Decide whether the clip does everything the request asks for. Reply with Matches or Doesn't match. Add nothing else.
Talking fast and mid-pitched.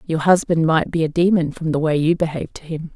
Matches